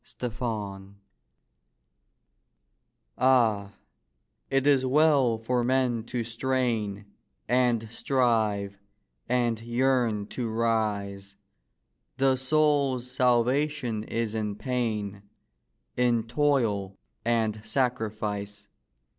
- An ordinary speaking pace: No, slow, 80 wpm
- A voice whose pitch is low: Yes, low, 115 Hz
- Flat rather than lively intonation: No, average, 3.2 semitones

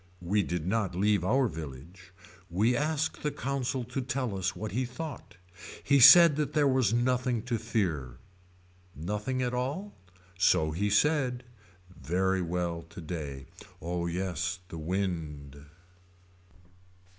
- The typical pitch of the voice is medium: No, low, 100 Hz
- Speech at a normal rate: No, slow, 130 wpm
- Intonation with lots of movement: Yes, wide, 6.7 semitones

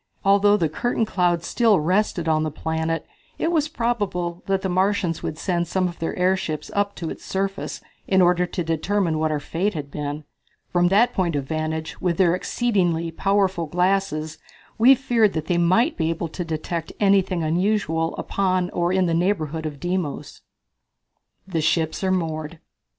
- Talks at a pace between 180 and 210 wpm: No, average, 170 wpm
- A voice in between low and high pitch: Yes, medium, 175 Hz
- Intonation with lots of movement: No, average, 3.3 semitones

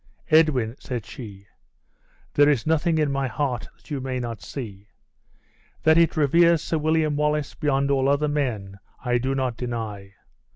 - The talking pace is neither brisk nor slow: Yes, average, 160 wpm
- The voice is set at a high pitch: No, low, 135 Hz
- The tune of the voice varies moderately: Yes, average, 4.1 semitones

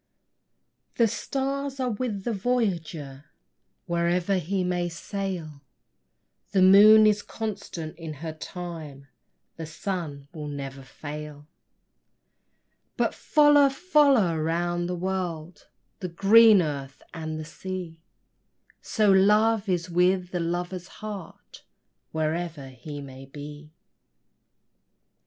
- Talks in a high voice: No, medium, 175 Hz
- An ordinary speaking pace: No, slow, 105 wpm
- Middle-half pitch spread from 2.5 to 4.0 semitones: No, average, 4.5 semitones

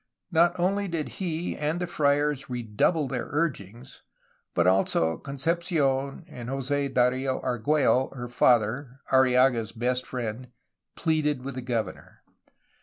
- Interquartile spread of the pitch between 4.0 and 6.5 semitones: No, average, 3.6 semitones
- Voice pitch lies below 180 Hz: Yes, low, 135 Hz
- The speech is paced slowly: Yes, slow, 120 wpm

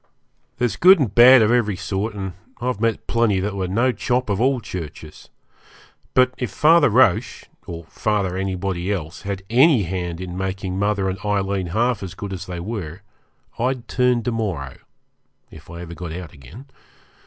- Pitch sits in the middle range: No, low, 100 Hz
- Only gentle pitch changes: No, average, 4.6 semitones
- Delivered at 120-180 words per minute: Yes, average, 175 wpm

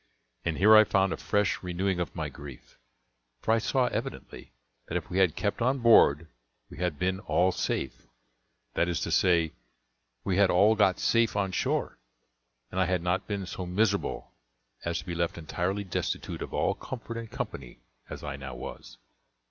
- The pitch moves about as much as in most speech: Yes, average, 3.2 semitones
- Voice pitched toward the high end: No, very low, 95 Hz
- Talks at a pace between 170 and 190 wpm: Yes, average, 180 wpm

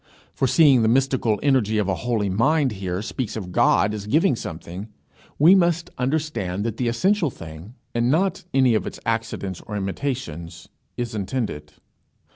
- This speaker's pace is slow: No, average, 160 wpm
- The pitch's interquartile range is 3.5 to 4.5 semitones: No, average, 5.3 semitones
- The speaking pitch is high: No, low, 115 Hz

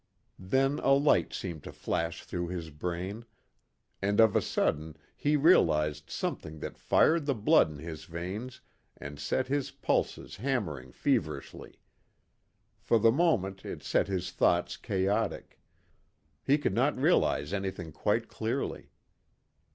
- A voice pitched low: Yes, very low, 95 Hz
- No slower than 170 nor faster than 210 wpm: No, slow, 135 wpm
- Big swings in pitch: Yes, wide, 8.1 semitones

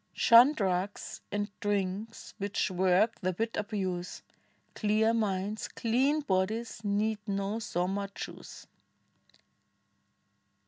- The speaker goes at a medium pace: No, slow, 95 wpm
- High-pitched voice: Yes, high, 205 Hz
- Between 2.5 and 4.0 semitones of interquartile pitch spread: Yes, average, 2.8 semitones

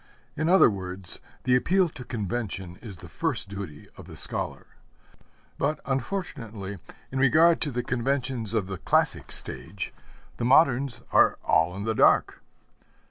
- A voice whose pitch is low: Yes, low, 120 Hz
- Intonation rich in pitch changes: Yes, wide, 5.9 semitones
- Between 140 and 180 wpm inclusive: Yes, average, 145 wpm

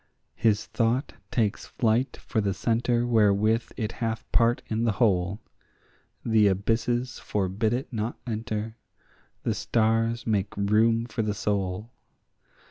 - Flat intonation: Yes, narrow, 1.9 semitones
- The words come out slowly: Yes, slow, 130 wpm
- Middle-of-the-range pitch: No, low, 110 Hz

